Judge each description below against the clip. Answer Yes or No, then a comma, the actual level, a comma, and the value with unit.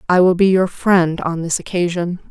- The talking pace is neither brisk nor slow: No, fast, 210 wpm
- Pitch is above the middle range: No, medium, 180 Hz